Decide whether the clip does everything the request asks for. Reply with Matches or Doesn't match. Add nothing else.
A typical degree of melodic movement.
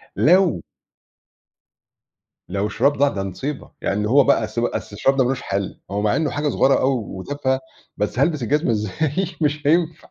Doesn't match